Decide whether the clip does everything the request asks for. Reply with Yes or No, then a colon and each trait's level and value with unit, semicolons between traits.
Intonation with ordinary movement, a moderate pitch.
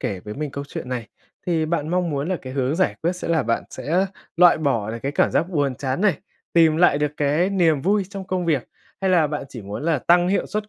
Yes: average, 4.4 semitones; medium, 155 Hz